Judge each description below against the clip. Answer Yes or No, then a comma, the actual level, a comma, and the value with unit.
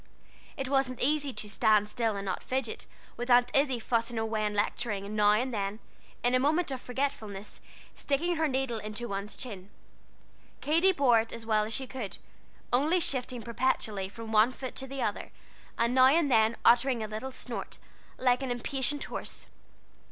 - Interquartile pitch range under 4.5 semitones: Yes, average, 3.6 semitones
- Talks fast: No, average, 180 wpm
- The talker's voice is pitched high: Yes, high, 245 Hz